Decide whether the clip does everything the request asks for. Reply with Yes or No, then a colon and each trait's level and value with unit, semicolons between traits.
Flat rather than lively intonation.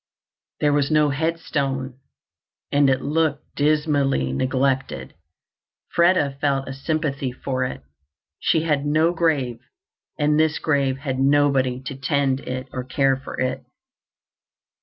Yes: narrow, 2.1 semitones